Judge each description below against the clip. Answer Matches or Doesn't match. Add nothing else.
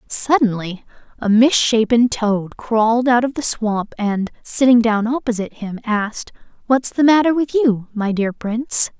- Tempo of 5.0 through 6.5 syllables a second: Doesn't match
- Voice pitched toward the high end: Matches